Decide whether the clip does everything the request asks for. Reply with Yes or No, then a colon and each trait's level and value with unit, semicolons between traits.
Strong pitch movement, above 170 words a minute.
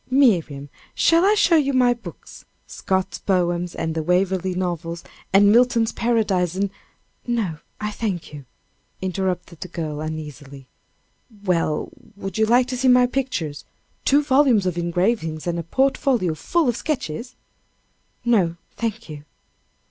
No: wide, 6.3 semitones; average, 140 wpm